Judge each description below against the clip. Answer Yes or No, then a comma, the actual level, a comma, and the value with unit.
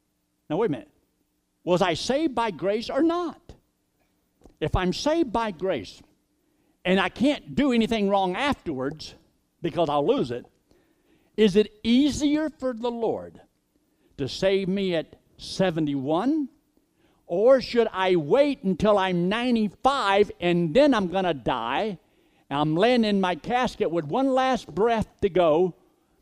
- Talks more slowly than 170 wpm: Yes, average, 145 wpm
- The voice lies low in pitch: No, high, 210 Hz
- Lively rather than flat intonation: Yes, wide, 6.2 semitones